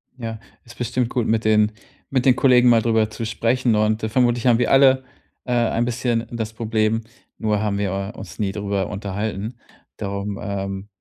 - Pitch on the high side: No, low, 110 Hz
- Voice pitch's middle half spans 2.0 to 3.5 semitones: Yes, narrow, 2.6 semitones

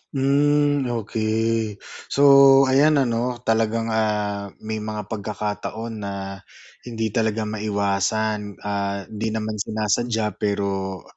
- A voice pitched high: No, low, 110 Hz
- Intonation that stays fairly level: Yes, narrow, 1.8 semitones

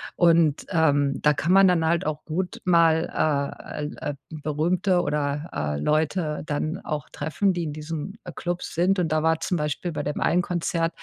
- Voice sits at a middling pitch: Yes, medium, 160 Hz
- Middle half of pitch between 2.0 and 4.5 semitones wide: Yes, average, 2.7 semitones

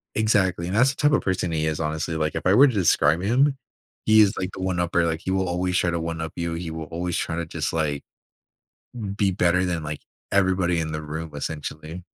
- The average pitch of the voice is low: Yes, very low, 85 Hz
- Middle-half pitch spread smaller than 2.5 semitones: No, average, 2.8 semitones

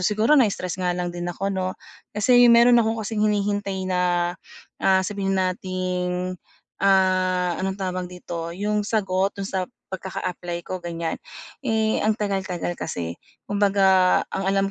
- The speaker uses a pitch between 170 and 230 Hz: Yes, high, 190 Hz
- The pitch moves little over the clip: Yes, narrow, 2.2 semitones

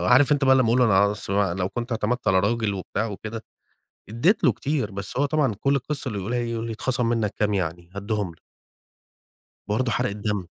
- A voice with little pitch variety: No, average, 3.9 semitones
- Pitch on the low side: Yes, low, 110 Hz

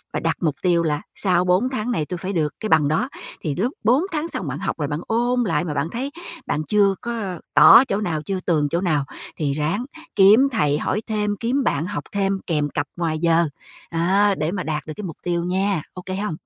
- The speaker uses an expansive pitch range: No, average, 5.0 semitones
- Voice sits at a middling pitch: Yes, medium, 180 Hz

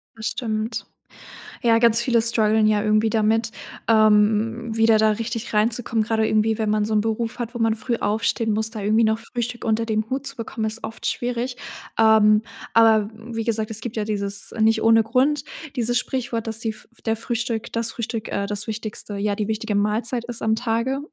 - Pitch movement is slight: Yes, narrow, 1.3 semitones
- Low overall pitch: No, high, 225 Hz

